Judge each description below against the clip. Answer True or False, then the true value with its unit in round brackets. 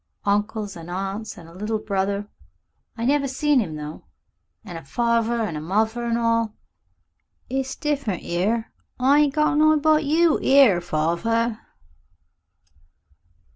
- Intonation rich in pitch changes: True (5.7 semitones)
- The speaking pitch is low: False (225 Hz)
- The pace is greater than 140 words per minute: False (135 wpm)